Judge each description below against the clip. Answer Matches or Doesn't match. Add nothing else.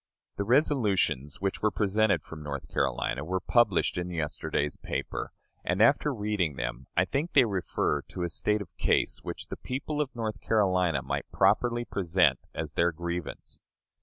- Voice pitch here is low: Matches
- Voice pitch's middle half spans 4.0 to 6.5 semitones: Matches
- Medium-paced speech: Matches